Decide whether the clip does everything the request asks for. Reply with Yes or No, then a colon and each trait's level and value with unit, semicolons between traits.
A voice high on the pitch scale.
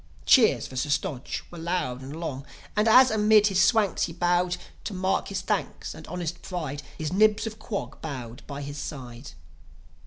No: medium, 175 Hz